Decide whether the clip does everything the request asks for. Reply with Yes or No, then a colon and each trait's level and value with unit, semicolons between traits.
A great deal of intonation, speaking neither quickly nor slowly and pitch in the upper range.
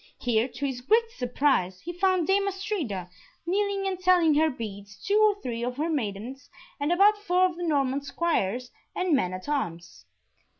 Yes: wide, 7.5 semitones; average, 175 wpm; very high, 295 Hz